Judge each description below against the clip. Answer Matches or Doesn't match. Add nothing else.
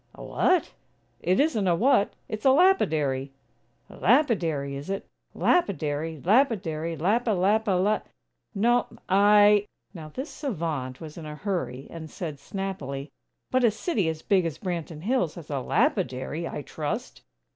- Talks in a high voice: Doesn't match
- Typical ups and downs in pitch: Doesn't match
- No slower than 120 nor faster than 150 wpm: Matches